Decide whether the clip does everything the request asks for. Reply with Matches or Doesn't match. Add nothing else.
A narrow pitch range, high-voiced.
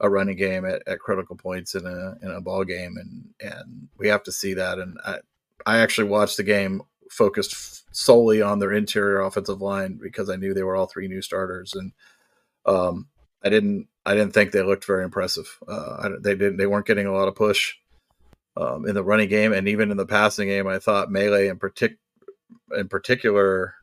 Doesn't match